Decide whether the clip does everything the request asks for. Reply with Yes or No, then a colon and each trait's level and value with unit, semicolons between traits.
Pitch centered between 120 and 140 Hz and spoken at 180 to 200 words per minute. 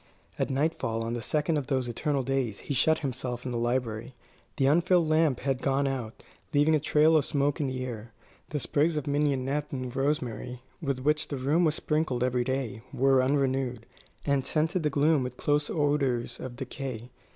Yes: low, 135 Hz; average, 185 wpm